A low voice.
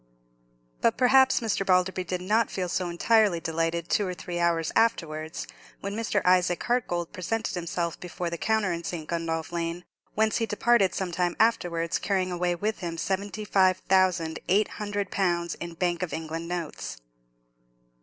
No: medium, 180 Hz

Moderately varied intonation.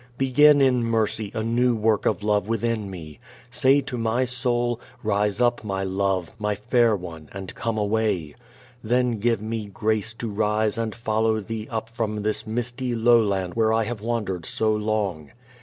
No: narrow, 2.2 semitones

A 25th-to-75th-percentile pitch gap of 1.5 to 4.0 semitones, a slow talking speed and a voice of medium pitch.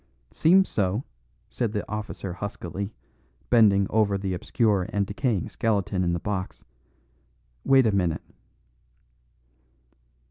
No: average, 2.8 semitones; slow, 110 wpm; low, 100 Hz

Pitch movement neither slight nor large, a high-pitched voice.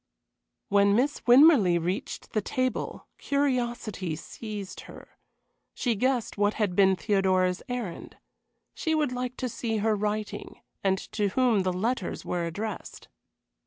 Yes: average, 4.6 semitones; high, 210 Hz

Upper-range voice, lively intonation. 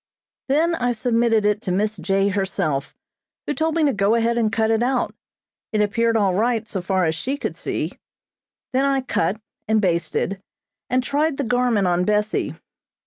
No: high, 220 Hz; average, 4.2 semitones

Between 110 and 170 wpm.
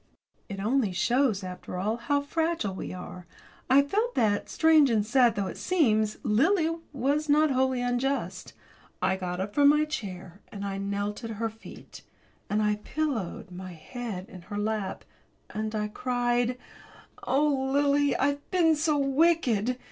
Yes: average, 155 wpm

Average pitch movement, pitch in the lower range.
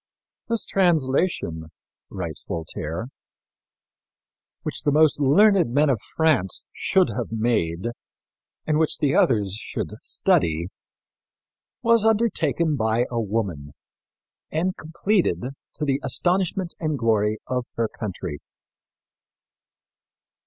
No: wide, 8.3 semitones; low, 130 Hz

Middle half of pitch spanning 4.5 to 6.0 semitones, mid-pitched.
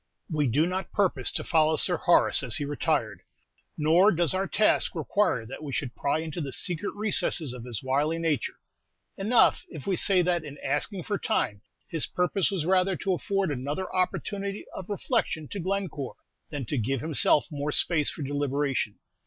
Yes: average, 4.8 semitones; medium, 160 Hz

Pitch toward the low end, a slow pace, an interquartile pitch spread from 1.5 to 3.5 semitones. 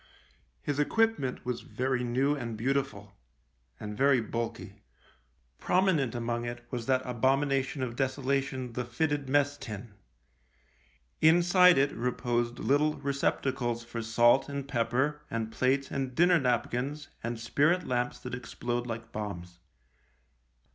Yes: low, 130 Hz; slow, 130 wpm; average, 2.9 semitones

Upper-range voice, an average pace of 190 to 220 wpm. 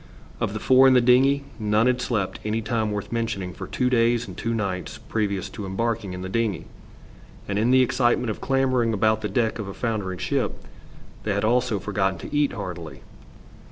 No: low, 110 Hz; average, 195 wpm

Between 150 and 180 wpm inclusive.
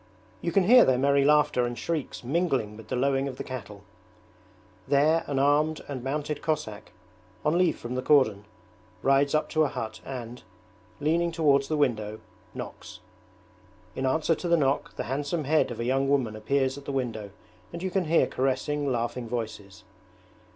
Yes: average, 175 wpm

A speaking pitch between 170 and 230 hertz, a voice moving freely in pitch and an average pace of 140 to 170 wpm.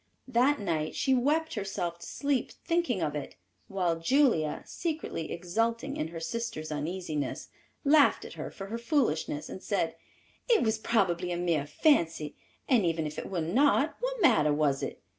Yes: high, 190 Hz; wide, 8.4 semitones; average, 165 wpm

